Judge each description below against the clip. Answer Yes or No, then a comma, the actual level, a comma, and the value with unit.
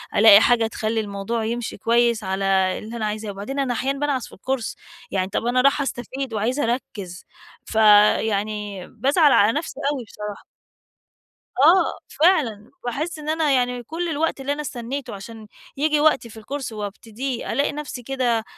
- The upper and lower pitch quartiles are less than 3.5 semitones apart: No, average, 4.4 semitones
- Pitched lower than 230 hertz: No, high, 240 Hz